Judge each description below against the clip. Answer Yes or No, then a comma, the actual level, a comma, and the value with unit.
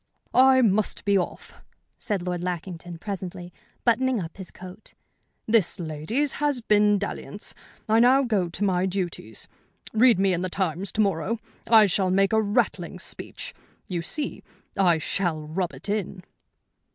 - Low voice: No, high, 195 Hz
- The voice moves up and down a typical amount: Yes, average, 3.6 semitones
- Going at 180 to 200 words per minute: No, average, 150 wpm